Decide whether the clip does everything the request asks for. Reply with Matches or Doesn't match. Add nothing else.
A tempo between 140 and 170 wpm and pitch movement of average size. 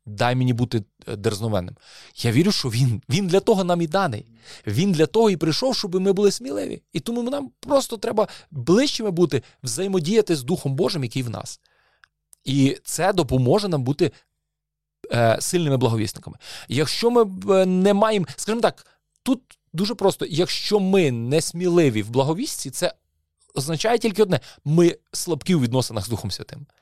Doesn't match